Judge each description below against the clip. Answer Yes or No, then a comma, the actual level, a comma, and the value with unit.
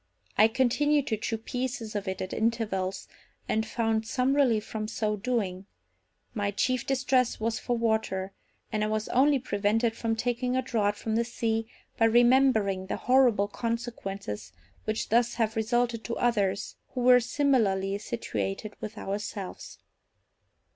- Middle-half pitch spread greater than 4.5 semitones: No, average, 2.9 semitones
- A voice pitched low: No, high, 225 Hz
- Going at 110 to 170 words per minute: Yes, average, 145 wpm